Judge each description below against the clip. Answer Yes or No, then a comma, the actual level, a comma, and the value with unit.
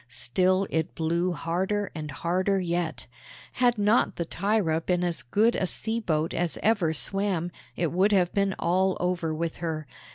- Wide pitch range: No, average, 3.2 semitones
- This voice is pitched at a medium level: Yes, medium, 180 Hz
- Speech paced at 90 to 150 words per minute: No, average, 165 wpm